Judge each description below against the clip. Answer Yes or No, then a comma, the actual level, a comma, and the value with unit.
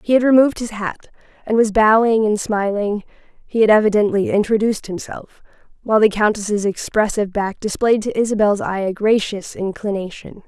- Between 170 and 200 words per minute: No, average, 155 wpm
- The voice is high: Yes, high, 210 Hz